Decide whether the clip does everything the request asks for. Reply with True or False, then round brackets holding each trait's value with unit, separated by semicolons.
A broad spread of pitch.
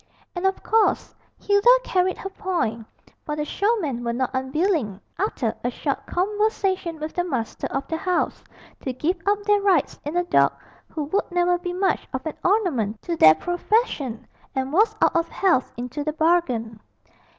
True (6.6 semitones)